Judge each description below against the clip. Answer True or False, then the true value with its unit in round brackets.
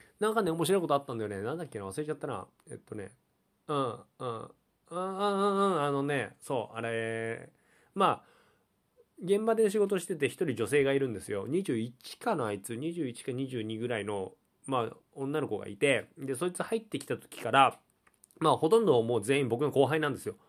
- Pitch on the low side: False (145 Hz)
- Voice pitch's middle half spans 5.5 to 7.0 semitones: False (7.9 semitones)